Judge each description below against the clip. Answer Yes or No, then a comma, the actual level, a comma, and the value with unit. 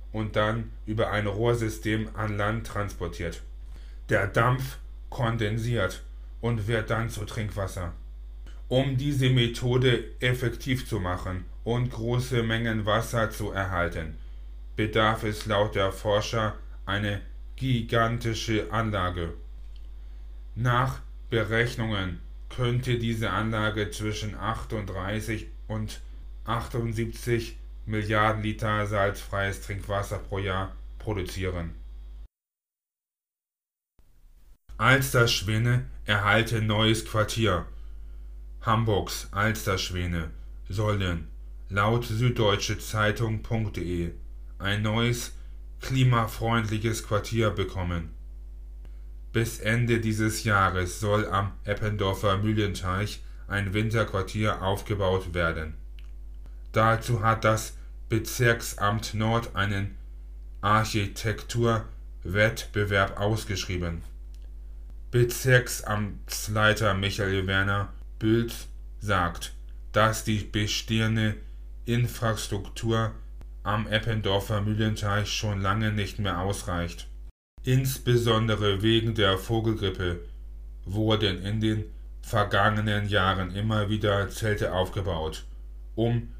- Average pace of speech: No, slow, 80 wpm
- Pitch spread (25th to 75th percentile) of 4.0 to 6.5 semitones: Yes, average, 4.4 semitones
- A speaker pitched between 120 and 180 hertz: No, low, 105 Hz